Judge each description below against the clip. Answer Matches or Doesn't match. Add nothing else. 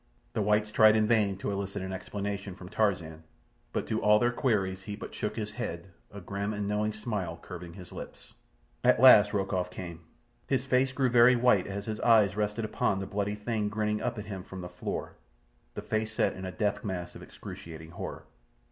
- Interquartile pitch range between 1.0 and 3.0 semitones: Matches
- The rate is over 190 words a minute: Matches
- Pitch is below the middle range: Matches